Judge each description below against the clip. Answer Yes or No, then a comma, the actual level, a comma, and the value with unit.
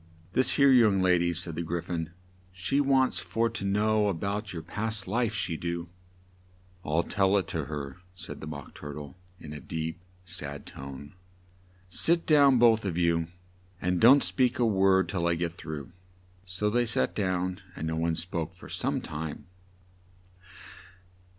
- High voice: No, very low, 90 Hz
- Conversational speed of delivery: Yes, average, 170 wpm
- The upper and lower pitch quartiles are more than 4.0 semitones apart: Yes, average, 4.9 semitones